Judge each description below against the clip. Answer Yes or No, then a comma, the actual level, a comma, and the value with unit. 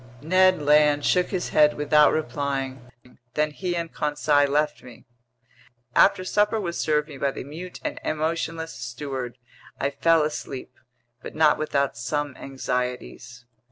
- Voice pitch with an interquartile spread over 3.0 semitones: No, average, 2.7 semitones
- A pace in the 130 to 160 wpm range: Yes, average, 140 wpm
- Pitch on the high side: No, medium, 150 Hz